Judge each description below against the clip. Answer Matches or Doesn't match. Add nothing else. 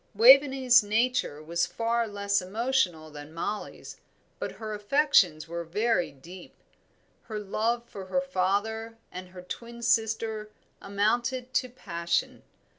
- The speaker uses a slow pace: Matches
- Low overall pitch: Doesn't match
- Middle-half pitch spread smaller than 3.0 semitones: Doesn't match